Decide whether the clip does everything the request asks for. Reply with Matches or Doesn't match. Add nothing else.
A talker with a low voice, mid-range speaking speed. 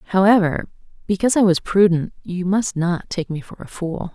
Doesn't match